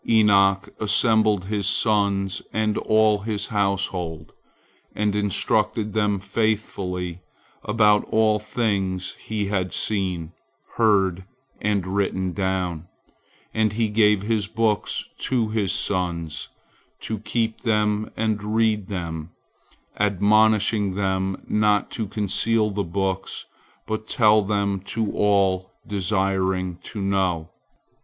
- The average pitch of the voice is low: Yes, low, 100 Hz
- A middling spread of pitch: No, narrow, 2.2 semitones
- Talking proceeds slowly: Yes, slow, 110 wpm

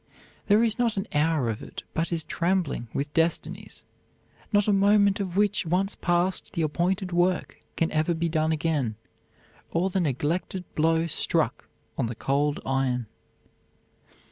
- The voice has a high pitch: No, medium, 170 Hz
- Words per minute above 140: Yes, average, 150 wpm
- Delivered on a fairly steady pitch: No, average, 4.1 semitones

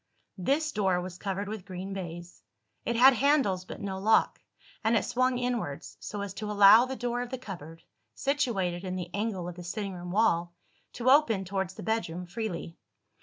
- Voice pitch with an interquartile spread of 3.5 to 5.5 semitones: Yes, average, 4.7 semitones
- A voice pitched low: No, high, 200 Hz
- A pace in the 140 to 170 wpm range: No, average, 185 wpm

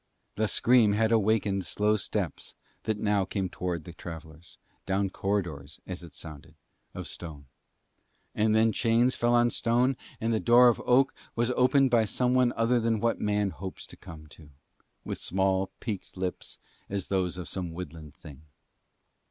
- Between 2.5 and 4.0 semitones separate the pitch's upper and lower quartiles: No, average, 4.8 semitones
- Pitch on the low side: Yes, low, 100 Hz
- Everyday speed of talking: Yes, average, 165 wpm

